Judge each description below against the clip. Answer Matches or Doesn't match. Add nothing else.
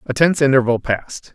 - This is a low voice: Matches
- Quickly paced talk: Doesn't match